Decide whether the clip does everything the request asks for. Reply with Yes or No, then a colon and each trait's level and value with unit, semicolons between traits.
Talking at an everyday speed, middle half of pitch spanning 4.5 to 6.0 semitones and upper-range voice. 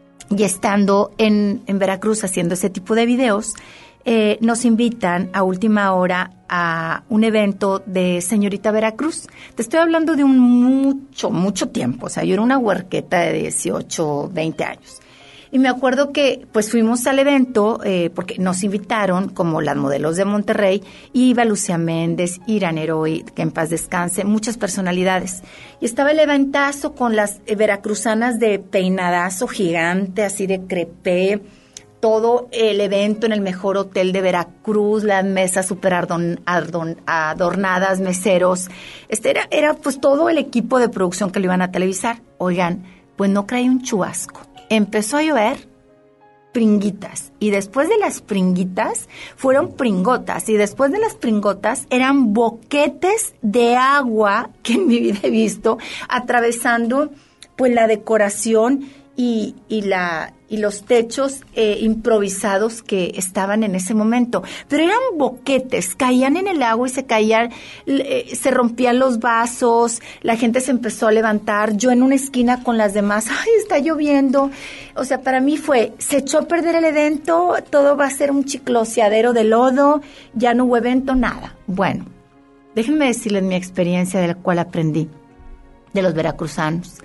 Yes: average, 155 wpm; average, 5.0 semitones; high, 220 Hz